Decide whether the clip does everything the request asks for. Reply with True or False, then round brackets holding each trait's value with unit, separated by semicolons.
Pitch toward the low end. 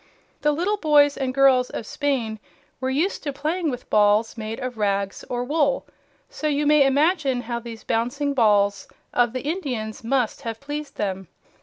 False (260 Hz)